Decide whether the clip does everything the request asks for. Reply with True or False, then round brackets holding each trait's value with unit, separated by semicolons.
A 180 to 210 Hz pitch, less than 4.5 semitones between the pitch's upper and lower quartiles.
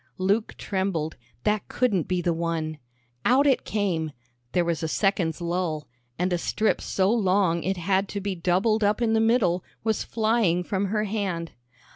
True (190 Hz; 3.8 semitones)